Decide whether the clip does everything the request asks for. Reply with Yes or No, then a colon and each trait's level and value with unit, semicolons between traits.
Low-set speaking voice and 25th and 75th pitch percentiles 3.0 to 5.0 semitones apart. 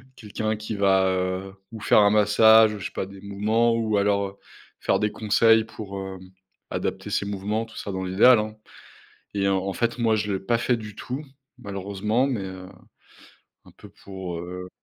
No: low, 105 Hz; narrow, 2.4 semitones